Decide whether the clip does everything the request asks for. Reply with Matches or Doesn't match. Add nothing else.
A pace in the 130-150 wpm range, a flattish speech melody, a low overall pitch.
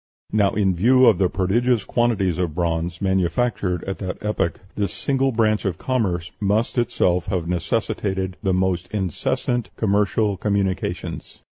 Doesn't match